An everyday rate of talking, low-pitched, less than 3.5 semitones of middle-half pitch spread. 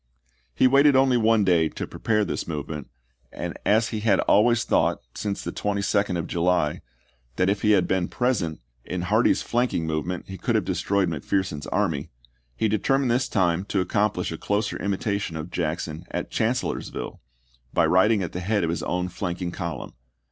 No: average, 185 wpm; very low, 95 Hz; average, 3.8 semitones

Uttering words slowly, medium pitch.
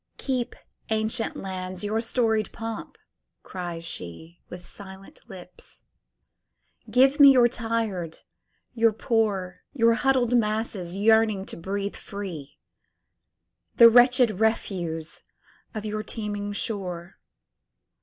No: slow, 95 wpm; high, 215 Hz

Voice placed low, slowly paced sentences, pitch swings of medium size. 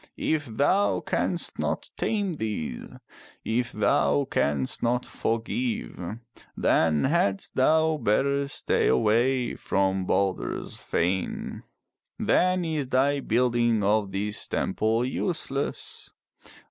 No: low, 120 Hz; slow, 100 wpm; wide, 6.4 semitones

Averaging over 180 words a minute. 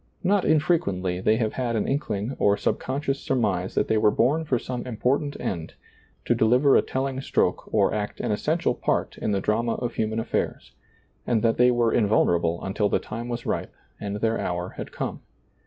Yes: average, 190 wpm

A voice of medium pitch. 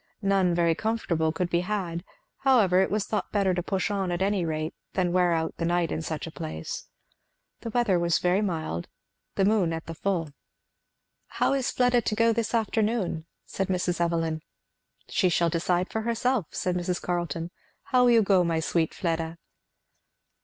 Yes: medium, 180 Hz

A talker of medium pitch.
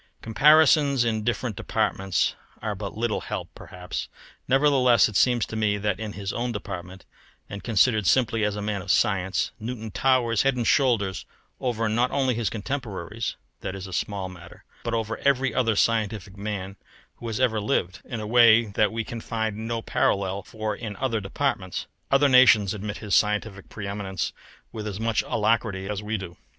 No: low, 110 Hz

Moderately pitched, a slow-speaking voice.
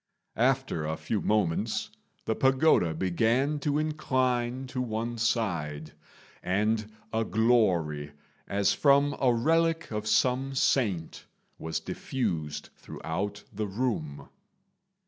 No: low, 110 Hz; slow, 105 wpm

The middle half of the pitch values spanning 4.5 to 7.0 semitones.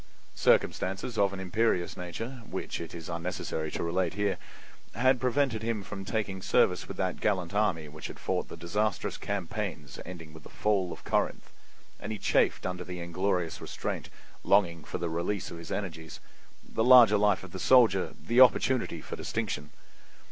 No: average, 3.9 semitones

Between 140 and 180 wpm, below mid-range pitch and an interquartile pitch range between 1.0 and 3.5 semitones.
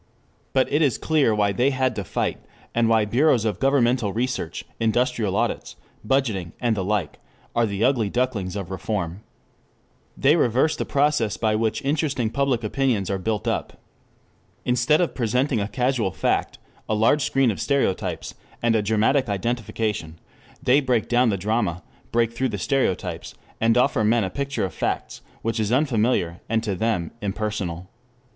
No: average, 165 wpm; low, 115 Hz; average, 4.0 semitones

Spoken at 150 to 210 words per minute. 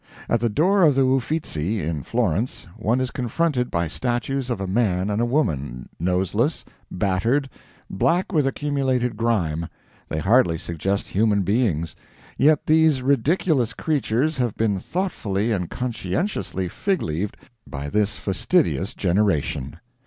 No: slow, 135 wpm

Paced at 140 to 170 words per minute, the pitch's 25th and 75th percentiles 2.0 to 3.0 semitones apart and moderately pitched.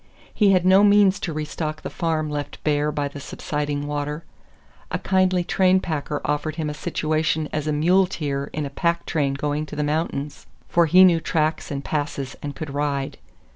No: average, 180 wpm; narrow, 2.5 semitones; medium, 155 Hz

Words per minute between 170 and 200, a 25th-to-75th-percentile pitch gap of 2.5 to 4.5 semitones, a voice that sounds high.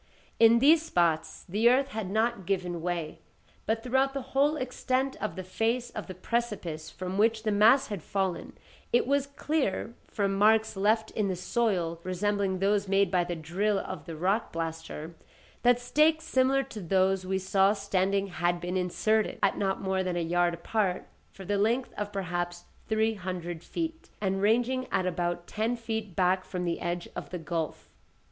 Yes: average, 180 wpm; average, 4.2 semitones; high, 195 Hz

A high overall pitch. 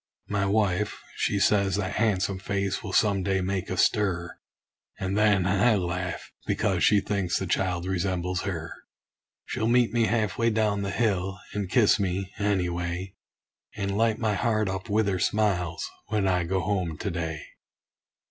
No: very low, 95 Hz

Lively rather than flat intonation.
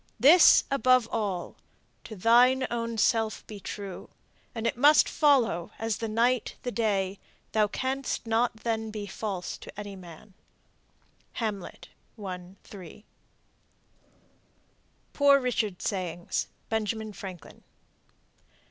No: average, 3.2 semitones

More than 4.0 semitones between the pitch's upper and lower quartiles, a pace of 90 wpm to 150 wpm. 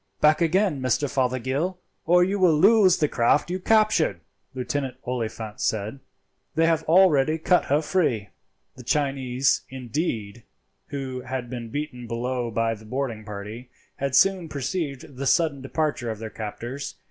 Yes: average, 5.0 semitones; average, 145 wpm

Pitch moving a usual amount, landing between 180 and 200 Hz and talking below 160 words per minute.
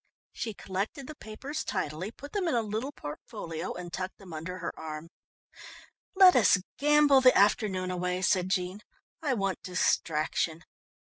No: wide, 6.3 semitones; high, 190 Hz; average, 150 wpm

